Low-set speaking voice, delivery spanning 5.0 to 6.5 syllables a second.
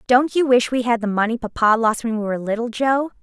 No: high, 235 Hz; 6.0 syllables/s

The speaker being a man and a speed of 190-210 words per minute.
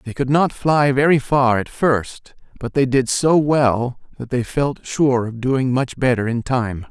Yes: male; average, 200 wpm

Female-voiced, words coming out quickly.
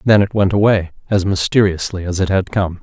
No: male; fast, 215 wpm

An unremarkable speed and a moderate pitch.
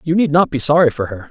No: fast, 320 wpm; medium, 150 Hz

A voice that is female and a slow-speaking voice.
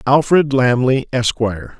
No: male; slow, 100 wpm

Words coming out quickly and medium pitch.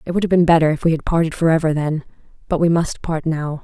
Yes: fast, 265 wpm; medium, 160 Hz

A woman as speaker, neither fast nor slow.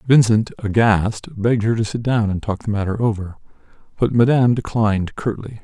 No: male; average, 170 wpm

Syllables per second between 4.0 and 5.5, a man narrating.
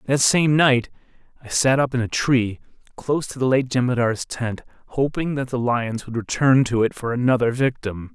Yes: 5.0 syllables/s; male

